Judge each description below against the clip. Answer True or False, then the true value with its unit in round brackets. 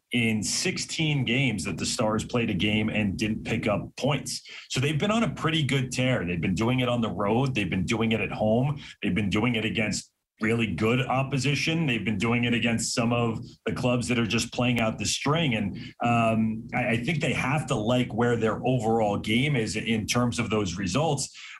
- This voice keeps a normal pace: False (215 wpm)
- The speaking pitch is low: True (120 Hz)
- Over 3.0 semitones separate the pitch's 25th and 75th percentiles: False (2.6 semitones)